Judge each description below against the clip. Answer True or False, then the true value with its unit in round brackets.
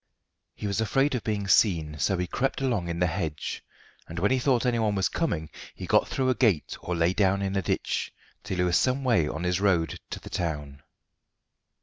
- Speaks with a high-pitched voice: False (95 Hz)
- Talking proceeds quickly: True (215 wpm)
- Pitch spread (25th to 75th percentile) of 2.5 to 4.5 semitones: False (5.5 semitones)